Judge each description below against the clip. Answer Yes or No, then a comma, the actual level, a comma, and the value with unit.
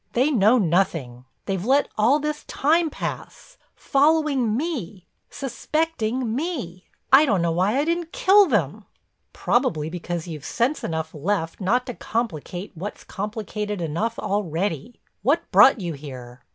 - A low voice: No, high, 210 Hz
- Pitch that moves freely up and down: Yes, wide, 8.0 semitones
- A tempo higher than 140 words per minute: No, slow, 135 wpm